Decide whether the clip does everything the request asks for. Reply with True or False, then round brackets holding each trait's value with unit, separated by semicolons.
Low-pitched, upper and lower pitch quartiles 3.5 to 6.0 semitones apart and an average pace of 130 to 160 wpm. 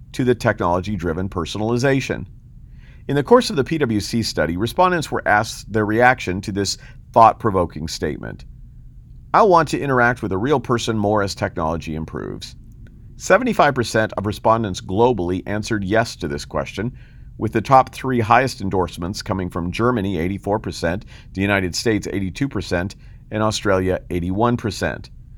True (105 Hz; 4.4 semitones; 140 wpm)